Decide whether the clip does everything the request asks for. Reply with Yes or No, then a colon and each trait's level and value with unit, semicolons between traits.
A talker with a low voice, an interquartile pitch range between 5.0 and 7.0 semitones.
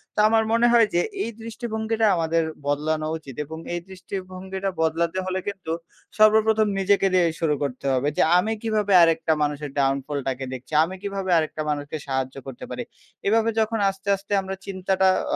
No: medium, 185 Hz; average, 5.3 semitones